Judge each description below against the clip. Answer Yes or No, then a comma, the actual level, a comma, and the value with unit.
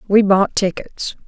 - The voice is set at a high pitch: Yes, high, 195 Hz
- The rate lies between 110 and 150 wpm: Yes, average, 140 wpm